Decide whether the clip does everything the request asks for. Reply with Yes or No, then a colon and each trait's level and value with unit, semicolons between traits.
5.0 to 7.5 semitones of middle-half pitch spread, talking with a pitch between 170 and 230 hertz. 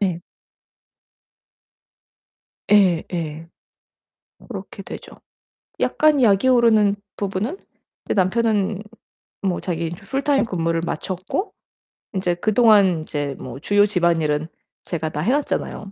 No: average, 4.5 semitones; high, 190 Hz